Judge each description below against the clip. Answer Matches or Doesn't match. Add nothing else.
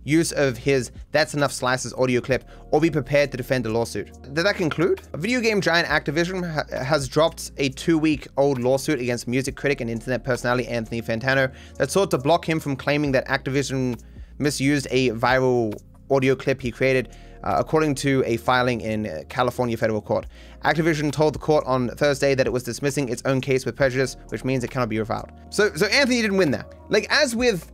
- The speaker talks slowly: Doesn't match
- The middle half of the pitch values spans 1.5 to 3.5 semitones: Doesn't match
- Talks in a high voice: Doesn't match